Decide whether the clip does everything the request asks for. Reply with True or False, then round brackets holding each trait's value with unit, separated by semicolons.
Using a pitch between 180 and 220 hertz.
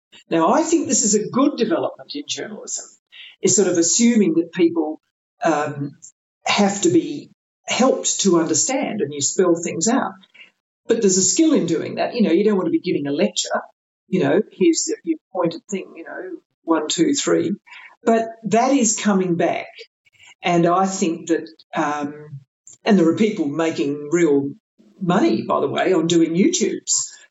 True (190 Hz)